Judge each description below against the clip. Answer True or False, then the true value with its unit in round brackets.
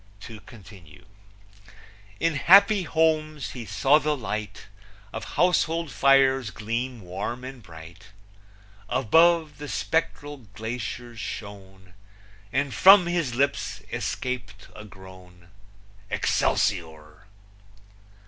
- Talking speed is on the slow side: True (95 wpm)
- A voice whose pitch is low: True (120 Hz)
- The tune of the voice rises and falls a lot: True (6.8 semitones)